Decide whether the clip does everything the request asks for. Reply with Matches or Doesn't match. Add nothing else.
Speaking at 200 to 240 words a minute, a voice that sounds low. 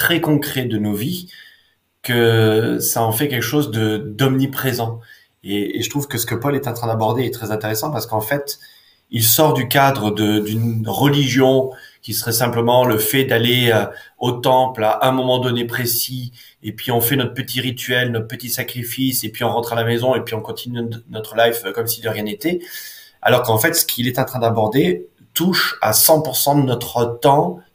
Matches